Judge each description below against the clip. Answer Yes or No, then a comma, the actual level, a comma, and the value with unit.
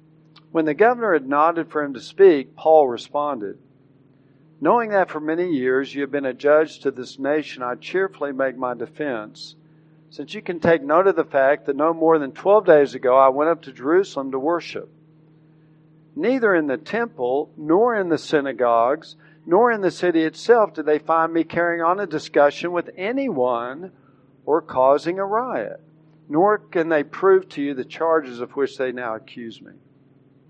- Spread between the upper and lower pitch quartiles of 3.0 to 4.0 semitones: Yes, average, 3.5 semitones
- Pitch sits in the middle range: Yes, medium, 155 Hz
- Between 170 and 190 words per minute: Yes, average, 180 wpm